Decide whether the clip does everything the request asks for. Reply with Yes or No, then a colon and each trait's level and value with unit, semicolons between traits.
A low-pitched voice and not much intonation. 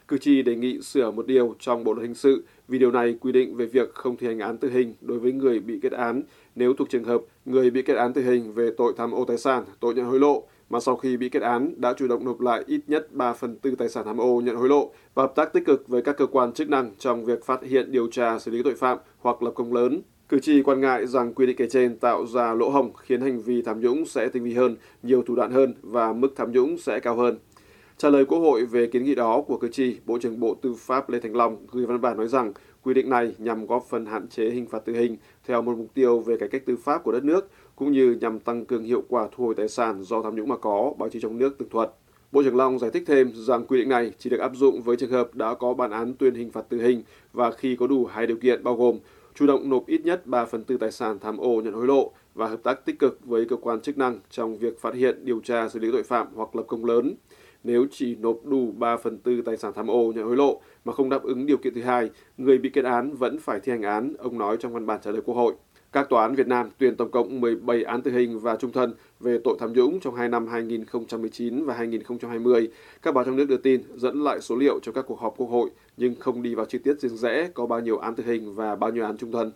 Yes: low, 120 Hz; narrow, 1.8 semitones